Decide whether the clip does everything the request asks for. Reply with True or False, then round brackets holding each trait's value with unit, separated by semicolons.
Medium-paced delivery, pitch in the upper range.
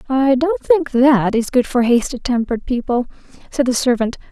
True (180 wpm; 255 Hz)